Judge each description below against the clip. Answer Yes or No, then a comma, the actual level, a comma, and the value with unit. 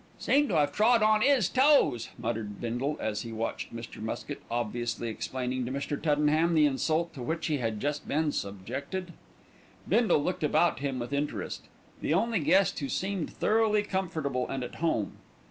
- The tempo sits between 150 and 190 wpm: Yes, average, 170 wpm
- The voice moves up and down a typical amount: No, wide, 7.1 semitones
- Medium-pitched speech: Yes, medium, 150 Hz